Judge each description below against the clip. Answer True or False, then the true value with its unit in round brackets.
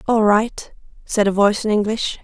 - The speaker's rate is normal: True (190 wpm)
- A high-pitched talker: True (210 Hz)